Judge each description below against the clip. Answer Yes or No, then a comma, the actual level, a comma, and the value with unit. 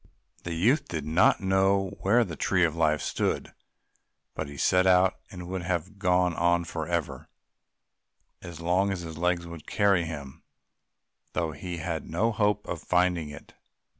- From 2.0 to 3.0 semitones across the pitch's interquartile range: Yes, narrow, 2.5 semitones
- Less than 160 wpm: No, average, 165 wpm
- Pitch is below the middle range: Yes, very low, 85 Hz